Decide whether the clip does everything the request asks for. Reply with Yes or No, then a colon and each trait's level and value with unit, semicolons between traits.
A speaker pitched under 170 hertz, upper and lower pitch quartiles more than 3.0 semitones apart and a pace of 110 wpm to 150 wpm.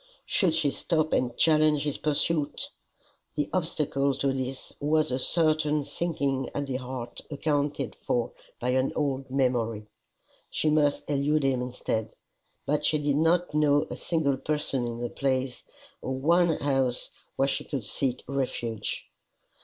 No: medium, 140 Hz; average, 2.7 semitones; average, 145 wpm